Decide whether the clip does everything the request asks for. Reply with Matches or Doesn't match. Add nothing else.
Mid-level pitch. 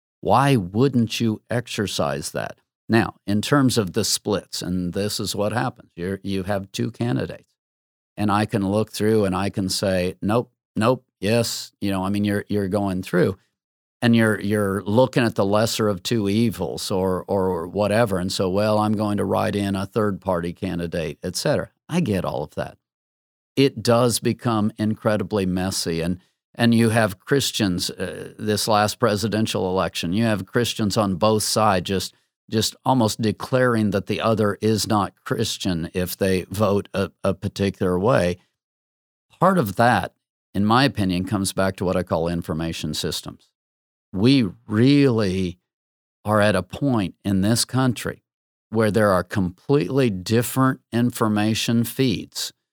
Doesn't match